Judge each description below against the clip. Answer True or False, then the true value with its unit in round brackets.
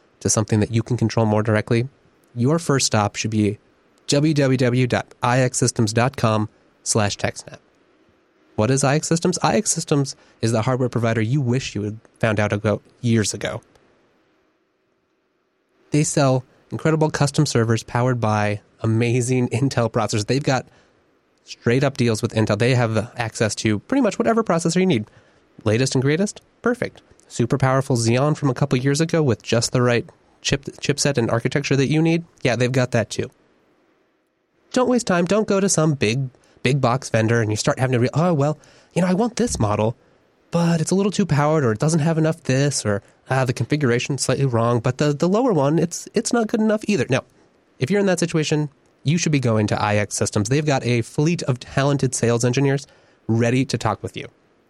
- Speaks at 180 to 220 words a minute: True (185 wpm)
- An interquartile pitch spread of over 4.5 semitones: True (5.1 semitones)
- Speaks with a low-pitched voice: True (130 Hz)